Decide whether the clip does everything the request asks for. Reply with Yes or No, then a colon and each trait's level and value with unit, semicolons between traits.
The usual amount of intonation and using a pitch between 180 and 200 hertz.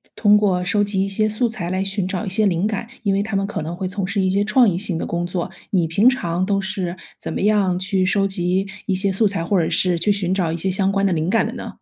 No: narrow, 2.2 semitones; high, 195 Hz